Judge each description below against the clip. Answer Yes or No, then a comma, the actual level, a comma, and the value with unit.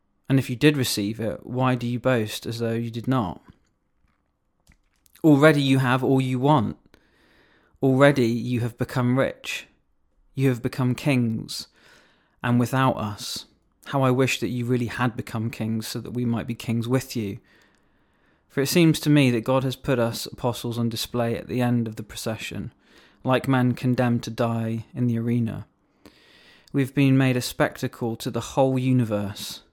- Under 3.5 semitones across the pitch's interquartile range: Yes, narrow, 2.6 semitones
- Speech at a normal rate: Yes, average, 175 wpm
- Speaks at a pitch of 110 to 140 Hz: Yes, low, 120 Hz